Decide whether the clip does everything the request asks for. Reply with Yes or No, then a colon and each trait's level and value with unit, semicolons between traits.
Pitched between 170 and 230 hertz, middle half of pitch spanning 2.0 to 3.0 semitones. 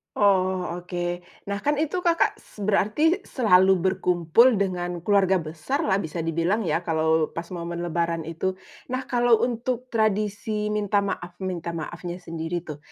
No: medium, 185 Hz; average, 3.8 semitones